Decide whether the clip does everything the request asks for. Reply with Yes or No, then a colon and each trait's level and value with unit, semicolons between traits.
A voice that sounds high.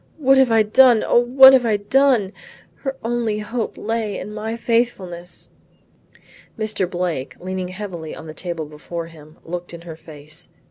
Yes: high, 205 Hz